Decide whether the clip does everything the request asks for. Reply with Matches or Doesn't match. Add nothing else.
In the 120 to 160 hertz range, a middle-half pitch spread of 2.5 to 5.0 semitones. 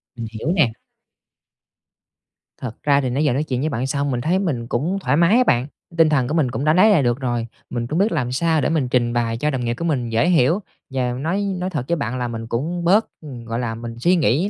Doesn't match